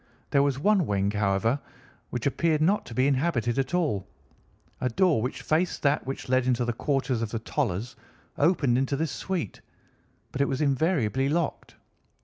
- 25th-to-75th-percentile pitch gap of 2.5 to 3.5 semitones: No, average, 4.5 semitones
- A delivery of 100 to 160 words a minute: No, average, 170 wpm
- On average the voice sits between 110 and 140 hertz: Yes, low, 135 Hz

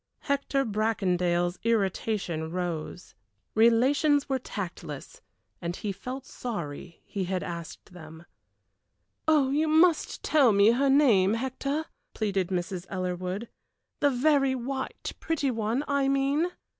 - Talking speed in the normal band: No, slow, 115 wpm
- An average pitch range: No, wide, 7.1 semitones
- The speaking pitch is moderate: No, high, 225 Hz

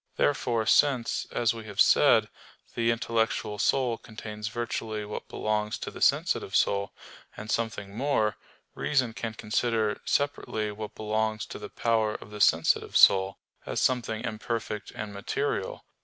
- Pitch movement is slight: Yes, narrow, 1.5 semitones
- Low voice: Yes, low, 110 Hz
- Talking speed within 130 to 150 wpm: Yes, average, 140 wpm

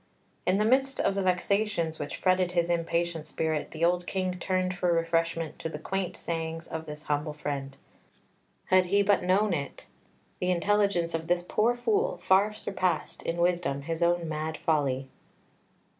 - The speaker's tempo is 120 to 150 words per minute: No, average, 165 wpm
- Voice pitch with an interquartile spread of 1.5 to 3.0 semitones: Yes, average, 2.7 semitones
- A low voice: No, medium, 175 Hz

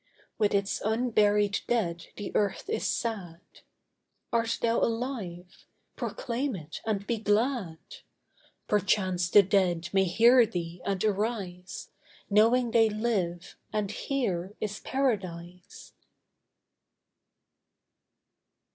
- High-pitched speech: Yes, high, 205 Hz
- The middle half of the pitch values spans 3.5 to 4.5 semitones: Yes, average, 4.1 semitones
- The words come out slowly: Yes, slow, 100 wpm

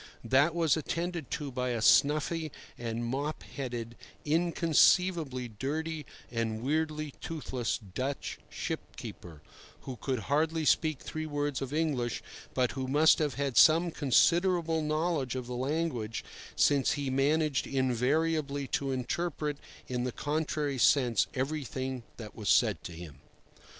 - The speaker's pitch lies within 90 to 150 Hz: Yes, medium, 140 Hz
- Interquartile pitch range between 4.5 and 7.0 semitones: No, average, 3.9 semitones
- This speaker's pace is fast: No, slow, 135 wpm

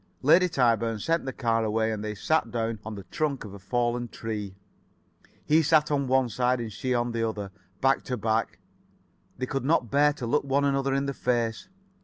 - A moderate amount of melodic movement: Yes, average, 3.5 semitones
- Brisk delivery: Yes, fast, 210 wpm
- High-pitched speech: No, low, 120 Hz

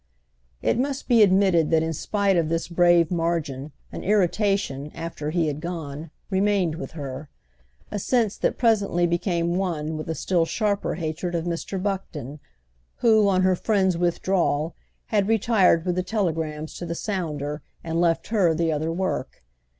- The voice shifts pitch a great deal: No, average, 3.4 semitones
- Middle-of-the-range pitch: Yes, medium, 175 Hz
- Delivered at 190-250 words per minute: No, average, 160 wpm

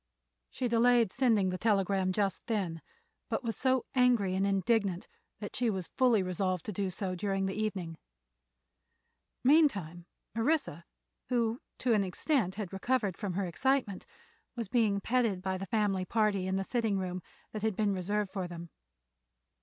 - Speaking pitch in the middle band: No, high, 200 Hz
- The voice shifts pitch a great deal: No, average, 3.7 semitones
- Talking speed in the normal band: Yes, average, 160 wpm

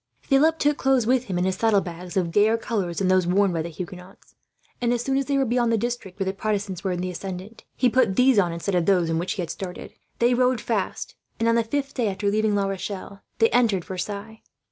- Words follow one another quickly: Yes, fast, 245 wpm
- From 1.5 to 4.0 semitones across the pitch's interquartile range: No, average, 4.5 semitones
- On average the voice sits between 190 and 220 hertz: Yes, high, 205 Hz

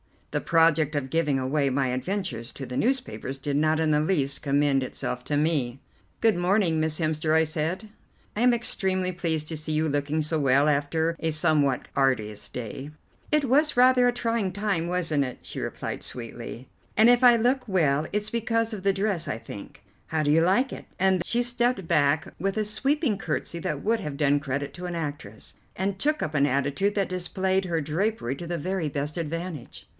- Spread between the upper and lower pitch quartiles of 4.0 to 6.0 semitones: Yes, wide, 5.5 semitones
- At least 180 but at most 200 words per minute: Yes, average, 195 wpm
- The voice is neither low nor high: Yes, medium, 160 Hz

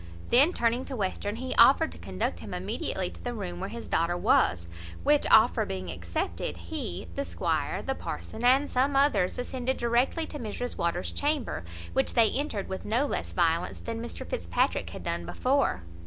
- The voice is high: Yes, high, 230 Hz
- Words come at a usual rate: Yes, average, 180 wpm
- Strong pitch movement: Yes, wide, 7.5 semitones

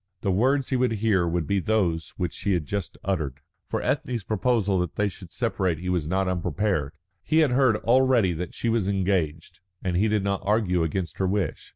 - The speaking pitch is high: No, very low, 95 Hz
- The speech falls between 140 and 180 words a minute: No, fast, 205 wpm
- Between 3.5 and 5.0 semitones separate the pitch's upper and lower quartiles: Yes, average, 4.0 semitones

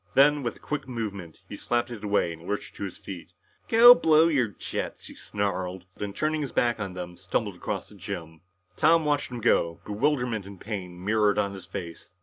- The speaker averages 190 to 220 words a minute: Yes, average, 200 wpm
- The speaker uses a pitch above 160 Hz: No, low, 105 Hz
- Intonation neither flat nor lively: No, wide, 5.7 semitones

